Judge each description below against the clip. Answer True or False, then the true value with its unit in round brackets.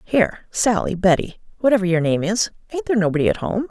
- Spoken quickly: False (160 wpm)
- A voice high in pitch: True (205 Hz)